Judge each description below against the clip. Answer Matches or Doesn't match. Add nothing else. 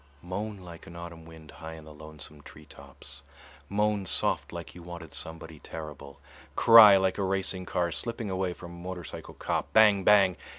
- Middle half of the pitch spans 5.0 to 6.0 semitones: Doesn't match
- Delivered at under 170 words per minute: Doesn't match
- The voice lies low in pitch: Matches